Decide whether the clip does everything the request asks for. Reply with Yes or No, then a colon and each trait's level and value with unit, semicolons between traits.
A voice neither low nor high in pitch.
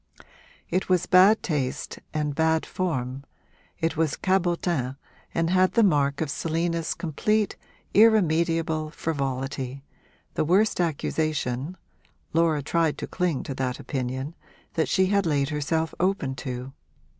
Yes: medium, 160 Hz